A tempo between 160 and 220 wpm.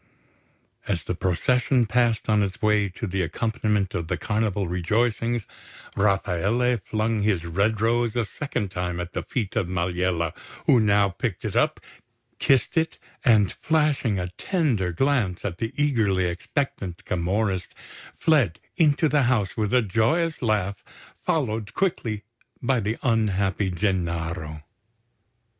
No: slow, 135 wpm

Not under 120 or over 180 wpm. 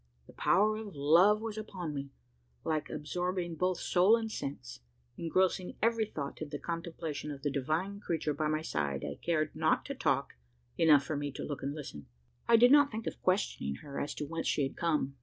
No: average, 200 wpm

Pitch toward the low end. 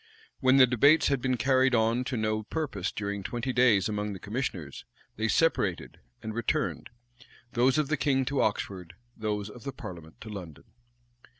Yes: low, 115 Hz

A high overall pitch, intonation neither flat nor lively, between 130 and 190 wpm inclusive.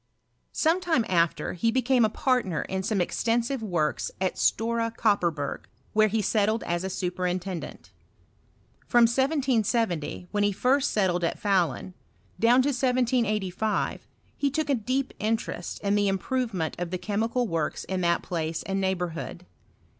Yes: high, 210 Hz; average, 5.0 semitones; average, 150 wpm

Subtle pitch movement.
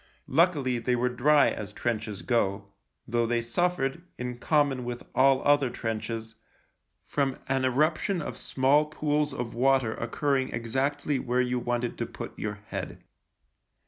No: average, 3.4 semitones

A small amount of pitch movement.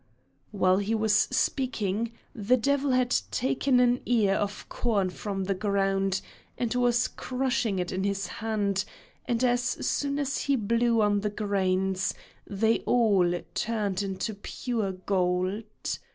No: average, 3.8 semitones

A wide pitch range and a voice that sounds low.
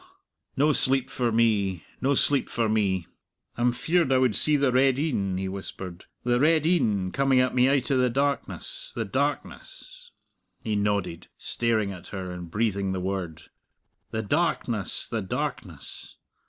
Yes: wide, 5.8 semitones; low, 115 Hz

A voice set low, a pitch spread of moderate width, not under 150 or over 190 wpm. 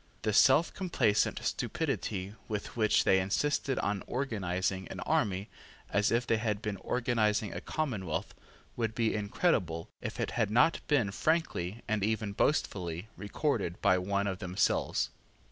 No: low, 105 Hz; average, 3.8 semitones; average, 140 wpm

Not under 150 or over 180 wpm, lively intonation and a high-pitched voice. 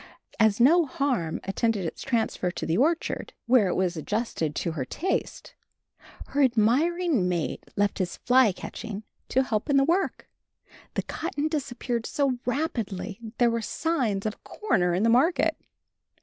Yes: average, 155 wpm; wide, 6.2 semitones; high, 235 Hz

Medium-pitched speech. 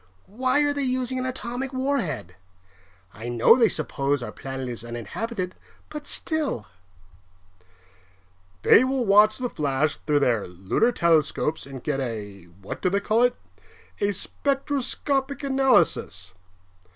Yes: medium, 170 Hz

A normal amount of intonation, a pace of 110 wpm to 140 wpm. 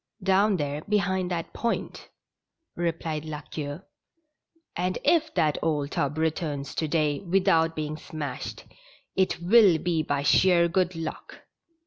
Yes: average, 3.5 semitones; slow, 135 wpm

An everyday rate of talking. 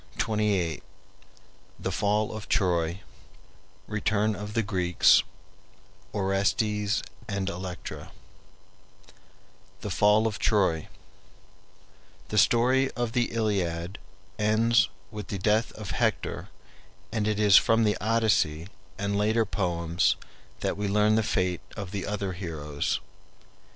No: slow, 115 wpm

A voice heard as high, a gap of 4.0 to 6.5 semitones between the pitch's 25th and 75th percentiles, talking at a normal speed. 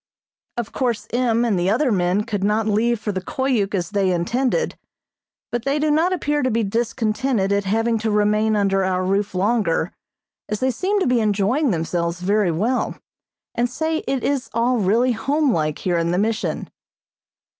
Yes: high, 220 Hz; average, 4.3 semitones; average, 180 wpm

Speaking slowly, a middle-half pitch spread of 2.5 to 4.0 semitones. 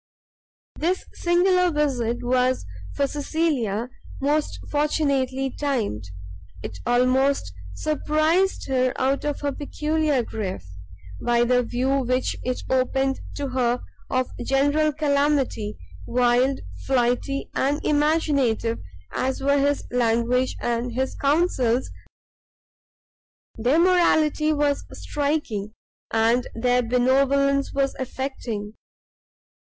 Yes: slow, 100 wpm; average, 3.1 semitones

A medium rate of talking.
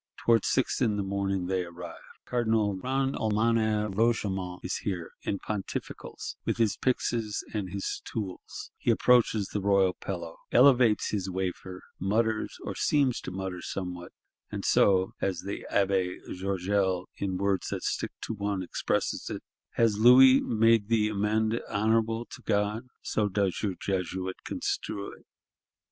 Yes: average, 145 wpm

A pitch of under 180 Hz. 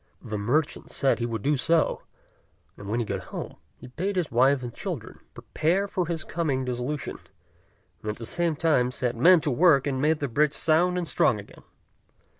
Yes: medium, 140 Hz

